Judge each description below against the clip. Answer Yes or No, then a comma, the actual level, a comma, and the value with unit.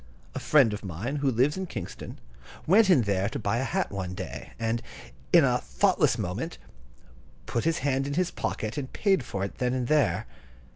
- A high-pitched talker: No, low, 130 Hz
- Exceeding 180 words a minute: Yes, average, 195 wpm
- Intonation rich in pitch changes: Yes, wide, 6.1 semitones